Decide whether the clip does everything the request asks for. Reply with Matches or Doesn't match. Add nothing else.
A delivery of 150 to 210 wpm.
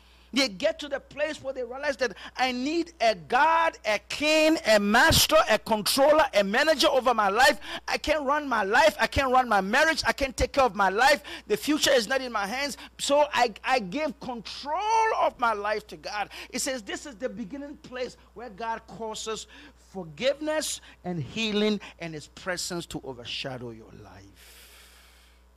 Matches